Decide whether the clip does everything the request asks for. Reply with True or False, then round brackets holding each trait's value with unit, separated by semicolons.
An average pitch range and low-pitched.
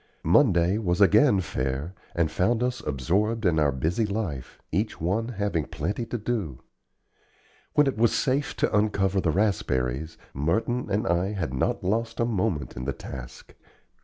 False (6.1 semitones; 95 Hz)